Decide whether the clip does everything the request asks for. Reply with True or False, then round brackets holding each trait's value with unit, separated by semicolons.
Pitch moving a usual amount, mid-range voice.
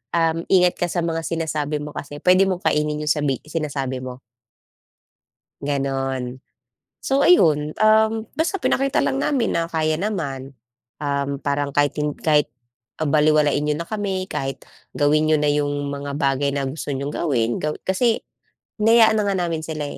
True (3.7 semitones; 150 Hz)